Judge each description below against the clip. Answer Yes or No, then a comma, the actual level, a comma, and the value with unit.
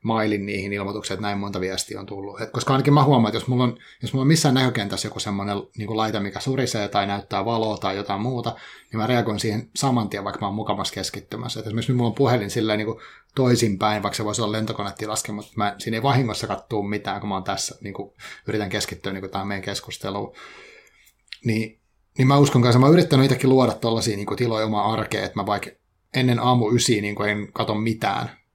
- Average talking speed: No, fast, 210 wpm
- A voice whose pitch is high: No, low, 110 Hz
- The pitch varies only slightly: No, average, 3.0 semitones